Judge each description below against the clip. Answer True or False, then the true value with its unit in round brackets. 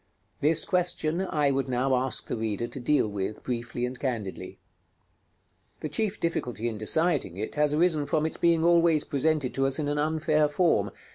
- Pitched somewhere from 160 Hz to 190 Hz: False (145 Hz)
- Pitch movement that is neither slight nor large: True (4.4 semitones)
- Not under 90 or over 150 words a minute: False (180 wpm)